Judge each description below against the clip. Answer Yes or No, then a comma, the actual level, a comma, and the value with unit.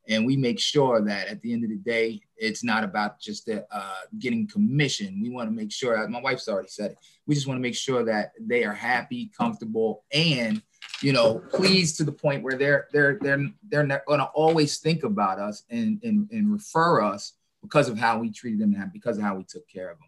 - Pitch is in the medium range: Yes, medium, 160 Hz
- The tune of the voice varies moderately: No, wide, 8.2 semitones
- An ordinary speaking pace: No, fast, 235 wpm